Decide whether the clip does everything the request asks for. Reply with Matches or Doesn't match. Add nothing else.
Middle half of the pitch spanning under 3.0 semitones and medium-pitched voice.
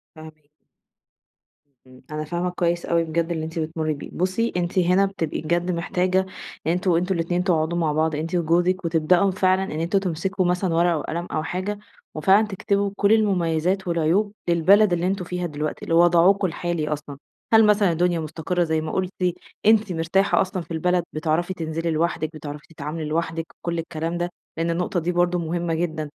Matches